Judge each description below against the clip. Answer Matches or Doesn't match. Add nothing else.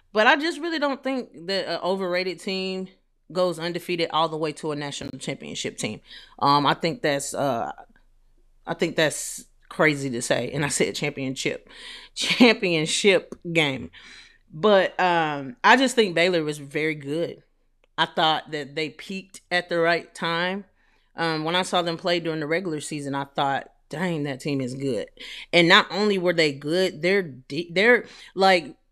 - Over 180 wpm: Doesn't match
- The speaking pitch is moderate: Matches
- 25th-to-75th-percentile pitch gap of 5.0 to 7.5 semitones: Doesn't match